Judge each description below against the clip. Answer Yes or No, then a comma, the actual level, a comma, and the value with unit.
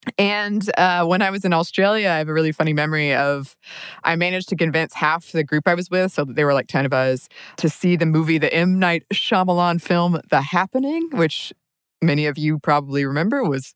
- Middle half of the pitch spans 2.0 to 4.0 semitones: Yes, average, 3.6 semitones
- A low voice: No, medium, 165 Hz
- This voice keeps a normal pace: No, fast, 220 wpm